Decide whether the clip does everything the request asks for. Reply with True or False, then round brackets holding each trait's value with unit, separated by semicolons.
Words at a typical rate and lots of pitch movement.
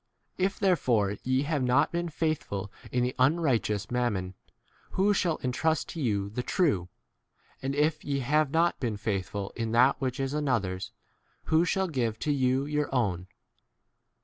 True (165 wpm; 6.0 semitones)